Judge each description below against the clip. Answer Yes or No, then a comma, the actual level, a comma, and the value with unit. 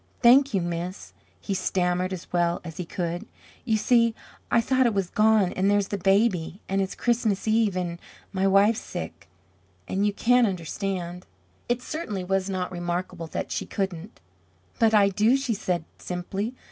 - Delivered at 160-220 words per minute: Yes, average, 170 wpm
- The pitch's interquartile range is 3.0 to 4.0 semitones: Yes, average, 3.7 semitones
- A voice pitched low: No, high, 195 Hz